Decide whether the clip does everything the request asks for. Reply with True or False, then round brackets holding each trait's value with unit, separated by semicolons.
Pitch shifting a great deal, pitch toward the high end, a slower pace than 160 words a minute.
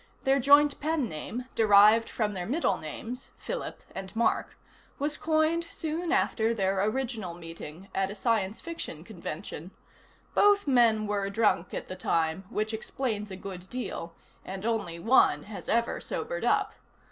True (5.8 semitones; 220 Hz; 150 wpm)